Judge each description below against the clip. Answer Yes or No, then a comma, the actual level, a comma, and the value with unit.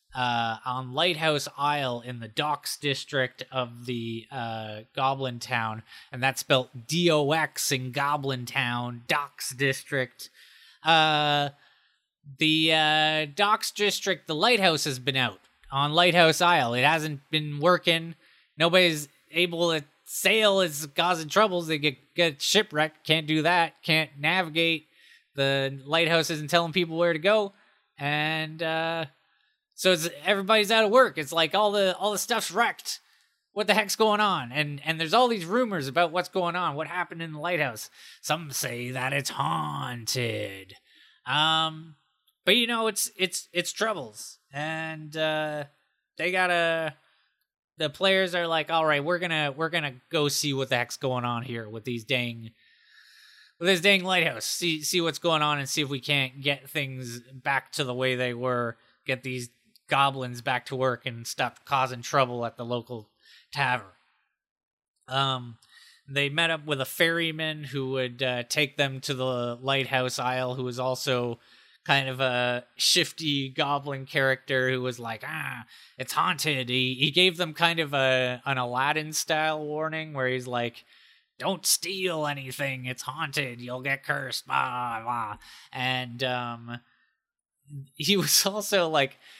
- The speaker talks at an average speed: Yes, average, 155 wpm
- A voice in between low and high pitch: Yes, medium, 150 Hz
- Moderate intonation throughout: Yes, average, 4.7 semitones